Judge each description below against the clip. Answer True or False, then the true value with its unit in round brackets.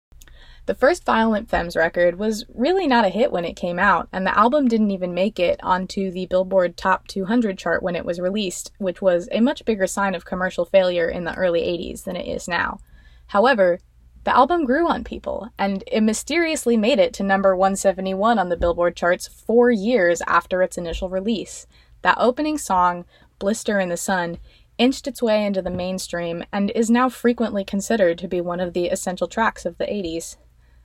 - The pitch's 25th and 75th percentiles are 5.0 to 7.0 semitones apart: False (4.3 semitones)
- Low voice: False (190 Hz)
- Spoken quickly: False (195 wpm)